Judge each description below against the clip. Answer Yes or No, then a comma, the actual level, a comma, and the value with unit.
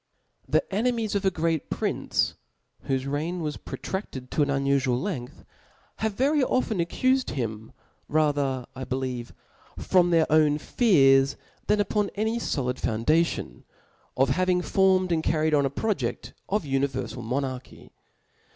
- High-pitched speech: No, medium, 155 Hz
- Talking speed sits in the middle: Yes, average, 150 wpm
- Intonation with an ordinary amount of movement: No, wide, 6.3 semitones